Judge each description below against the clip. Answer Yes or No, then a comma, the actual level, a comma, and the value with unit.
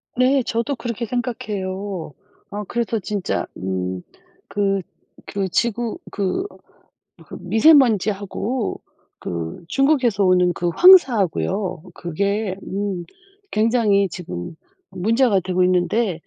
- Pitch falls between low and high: No, high, 200 Hz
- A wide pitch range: No, average, 4.3 semitones